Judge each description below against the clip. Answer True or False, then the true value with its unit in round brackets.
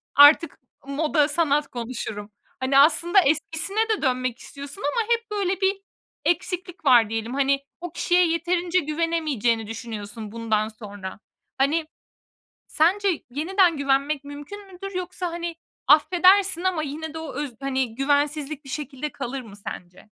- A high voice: True (295 Hz)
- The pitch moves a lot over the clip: False (5.0 semitones)